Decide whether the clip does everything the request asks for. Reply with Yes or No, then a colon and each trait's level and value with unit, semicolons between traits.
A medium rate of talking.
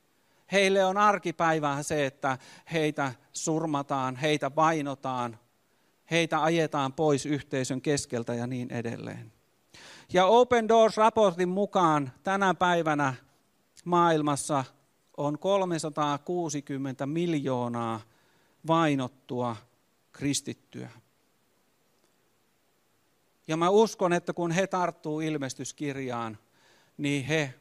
No: slow, 85 wpm